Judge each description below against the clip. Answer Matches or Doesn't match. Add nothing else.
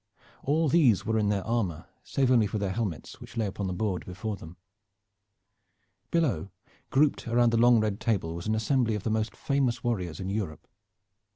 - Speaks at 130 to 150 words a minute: Doesn't match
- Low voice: Matches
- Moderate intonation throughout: Matches